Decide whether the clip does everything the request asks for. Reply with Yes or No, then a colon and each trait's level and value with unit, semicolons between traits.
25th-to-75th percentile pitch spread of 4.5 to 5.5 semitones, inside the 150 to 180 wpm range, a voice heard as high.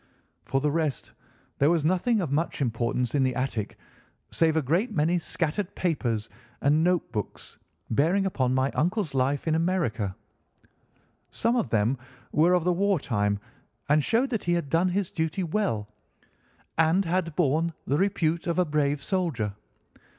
No: average, 5.0 semitones; average, 160 wpm; medium, 160 Hz